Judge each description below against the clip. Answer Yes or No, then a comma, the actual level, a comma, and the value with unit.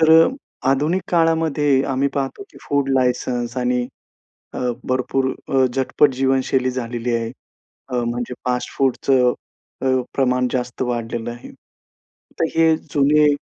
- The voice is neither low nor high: No, low, 130 Hz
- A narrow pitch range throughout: Yes, narrow, 2.2 semitones